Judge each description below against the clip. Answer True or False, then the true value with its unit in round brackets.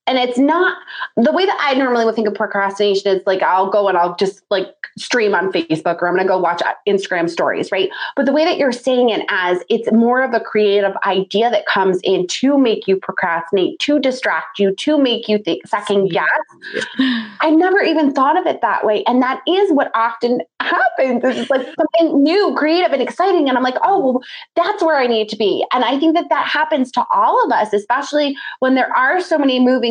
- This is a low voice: False (250 Hz)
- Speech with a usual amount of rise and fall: False (7.1 semitones)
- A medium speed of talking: False (220 wpm)